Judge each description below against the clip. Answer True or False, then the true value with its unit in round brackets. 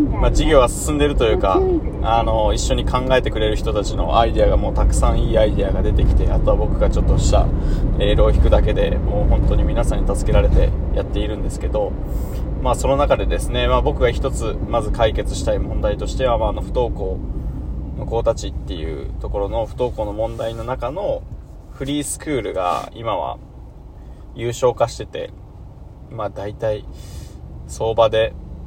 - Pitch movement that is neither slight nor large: False (6.3 semitones)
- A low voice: True (110 Hz)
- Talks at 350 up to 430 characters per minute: True (365 characters per minute)